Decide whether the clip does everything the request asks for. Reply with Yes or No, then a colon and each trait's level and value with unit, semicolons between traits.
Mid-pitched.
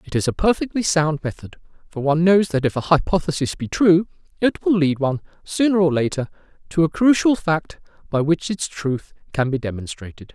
Yes: medium, 160 Hz